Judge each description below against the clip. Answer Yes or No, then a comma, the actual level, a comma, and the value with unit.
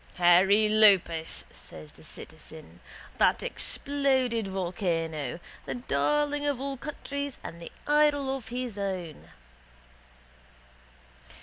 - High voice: Yes, high, 215 Hz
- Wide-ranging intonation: Yes, wide, 8.1 semitones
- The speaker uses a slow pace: Yes, slow, 100 wpm